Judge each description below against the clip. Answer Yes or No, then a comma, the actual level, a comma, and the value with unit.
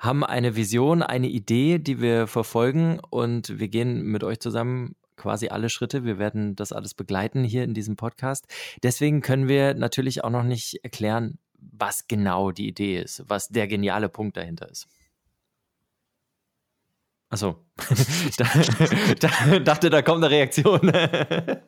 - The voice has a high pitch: No, low, 120 Hz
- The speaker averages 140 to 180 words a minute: Yes, average, 145 wpm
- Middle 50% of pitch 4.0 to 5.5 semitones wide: Yes, average, 4.9 semitones